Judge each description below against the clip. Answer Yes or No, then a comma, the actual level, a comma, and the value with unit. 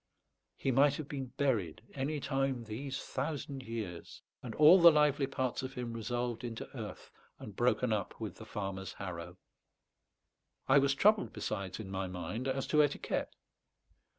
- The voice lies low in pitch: Yes, low, 130 Hz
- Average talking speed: Yes, average, 155 wpm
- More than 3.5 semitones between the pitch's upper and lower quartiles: Yes, average, 4.6 semitones